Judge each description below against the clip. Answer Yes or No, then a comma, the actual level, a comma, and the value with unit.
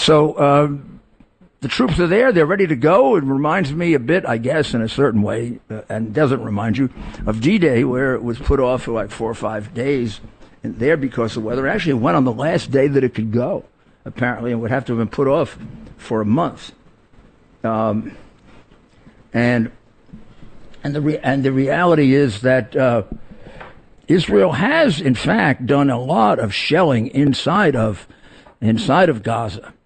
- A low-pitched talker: Yes, low, 125 Hz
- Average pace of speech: Yes, average, 185 wpm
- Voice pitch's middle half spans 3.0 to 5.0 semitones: Yes, average, 3.9 semitones